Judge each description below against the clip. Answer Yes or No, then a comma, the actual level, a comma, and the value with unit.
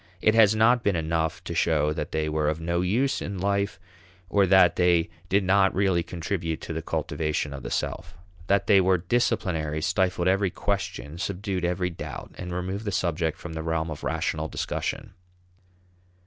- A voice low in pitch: Yes, very low, 90 Hz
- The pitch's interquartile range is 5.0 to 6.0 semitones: No, average, 3.3 semitones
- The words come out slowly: No, average, 175 wpm